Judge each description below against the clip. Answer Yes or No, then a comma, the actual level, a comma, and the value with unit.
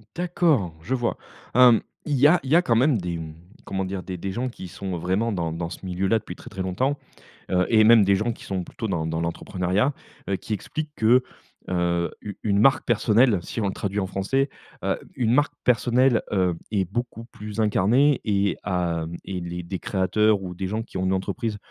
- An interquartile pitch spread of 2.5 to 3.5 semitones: No, average, 4.6 semitones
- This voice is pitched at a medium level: No, low, 100 Hz